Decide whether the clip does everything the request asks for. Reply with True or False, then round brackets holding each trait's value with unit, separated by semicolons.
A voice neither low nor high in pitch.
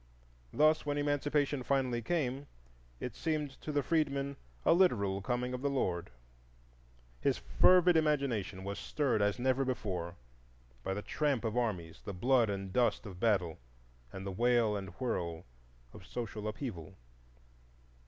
False (120 Hz)